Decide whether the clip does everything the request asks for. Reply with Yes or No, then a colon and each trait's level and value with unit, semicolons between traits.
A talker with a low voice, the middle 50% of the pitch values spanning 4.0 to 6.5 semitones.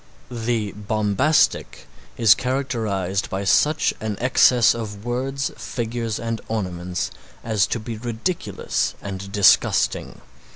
No: low, 110 Hz; average, 3.2 semitones